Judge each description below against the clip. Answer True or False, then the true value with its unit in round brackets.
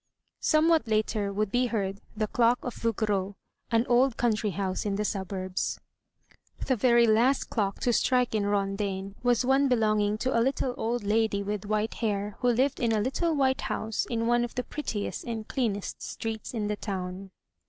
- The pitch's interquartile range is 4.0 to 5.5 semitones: False (3.2 semitones)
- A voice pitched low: False (220 Hz)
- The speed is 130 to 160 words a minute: False (180 wpm)